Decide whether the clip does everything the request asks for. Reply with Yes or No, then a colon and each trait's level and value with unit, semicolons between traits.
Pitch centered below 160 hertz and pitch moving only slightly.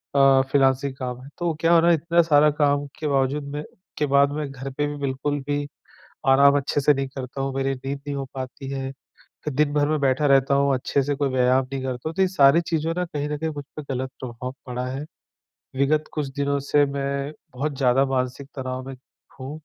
Yes: medium, 140 Hz; narrow, 1.8 semitones